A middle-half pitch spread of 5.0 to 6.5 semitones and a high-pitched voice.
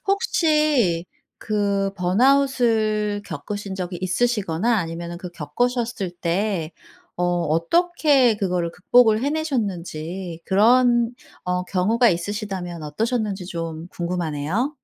Yes: wide, 5.5 semitones; high, 195 Hz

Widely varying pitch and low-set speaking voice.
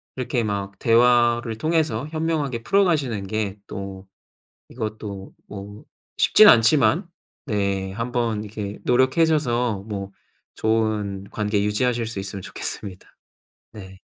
No: average, 3.7 semitones; low, 110 Hz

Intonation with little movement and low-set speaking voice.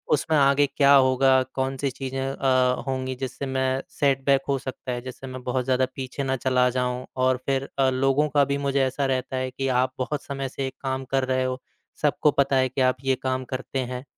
Yes: narrow, 0.9 semitones; low, 130 Hz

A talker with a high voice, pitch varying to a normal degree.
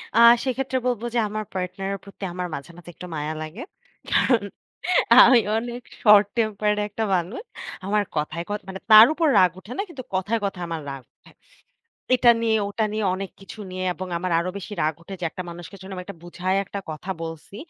Yes: high, 195 Hz; average, 3.6 semitones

